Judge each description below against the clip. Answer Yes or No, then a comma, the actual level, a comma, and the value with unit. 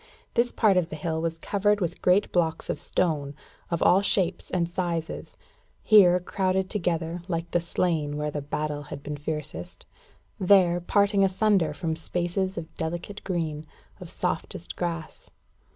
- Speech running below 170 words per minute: Yes, average, 150 wpm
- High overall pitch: No, medium, 170 Hz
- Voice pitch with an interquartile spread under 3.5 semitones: Yes, average, 2.8 semitones